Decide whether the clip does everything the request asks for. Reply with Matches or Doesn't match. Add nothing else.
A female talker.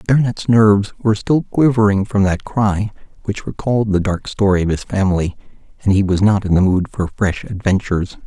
Doesn't match